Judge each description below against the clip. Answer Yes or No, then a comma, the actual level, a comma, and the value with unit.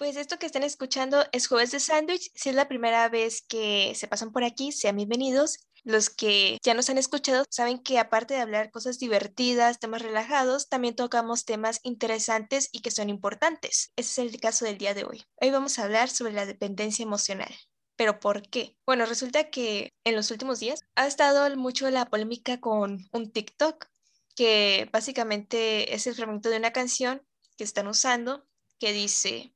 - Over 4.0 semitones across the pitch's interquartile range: No, average, 3.2 semitones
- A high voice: Yes, high, 235 Hz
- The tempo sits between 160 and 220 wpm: Yes, average, 185 wpm